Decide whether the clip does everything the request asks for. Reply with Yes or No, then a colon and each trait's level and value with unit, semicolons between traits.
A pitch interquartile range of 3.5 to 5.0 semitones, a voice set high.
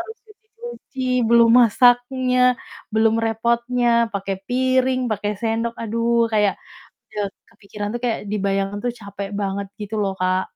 No: average, 3.1 semitones; high, 230 Hz